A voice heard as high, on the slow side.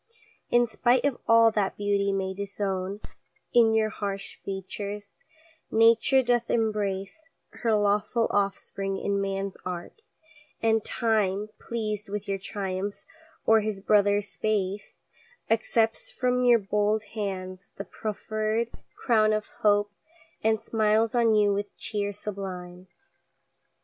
Yes: high, 210 Hz; slow, 120 wpm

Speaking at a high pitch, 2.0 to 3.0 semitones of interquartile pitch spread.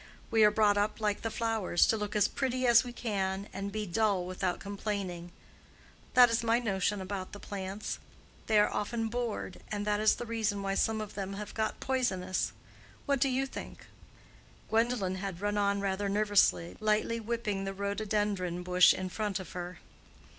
Yes: high, 205 Hz; narrow, 2.4 semitones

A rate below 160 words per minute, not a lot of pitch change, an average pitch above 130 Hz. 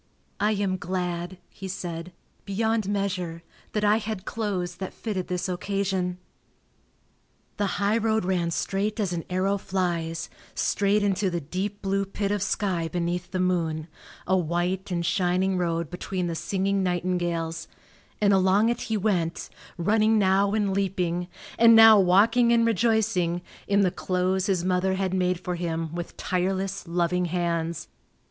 Yes: average, 150 wpm; narrow, 2.3 semitones; medium, 185 Hz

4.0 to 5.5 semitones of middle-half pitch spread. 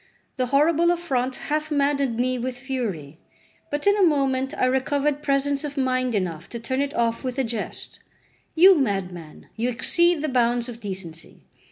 No: average, 3.6 semitones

